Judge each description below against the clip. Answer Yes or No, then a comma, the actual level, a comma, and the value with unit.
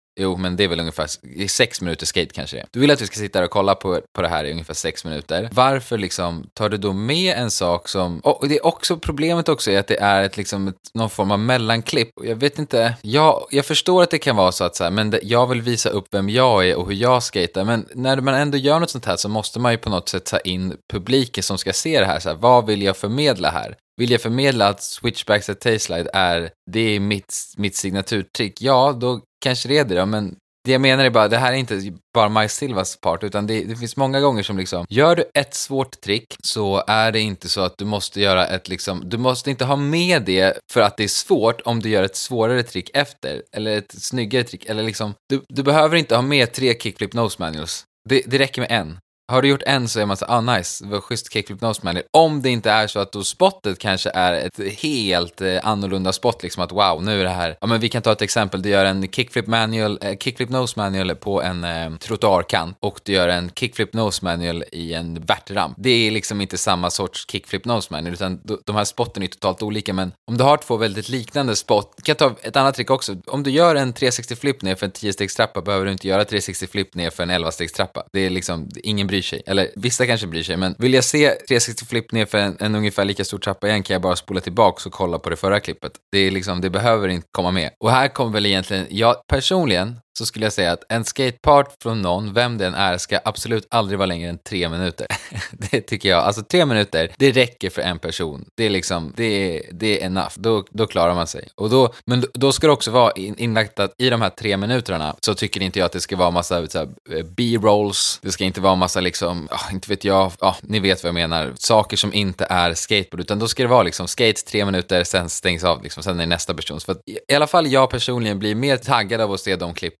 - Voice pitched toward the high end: No, low, 105 Hz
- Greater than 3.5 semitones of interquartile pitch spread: Yes, average, 4.5 semitones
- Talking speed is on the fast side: Yes, fast, 250 wpm